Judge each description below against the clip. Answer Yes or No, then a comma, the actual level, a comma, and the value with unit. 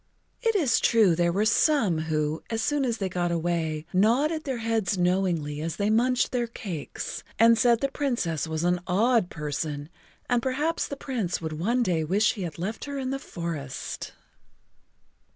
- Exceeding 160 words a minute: Yes, average, 175 wpm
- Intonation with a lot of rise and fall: Yes, wide, 6.6 semitones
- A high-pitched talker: Yes, high, 200 Hz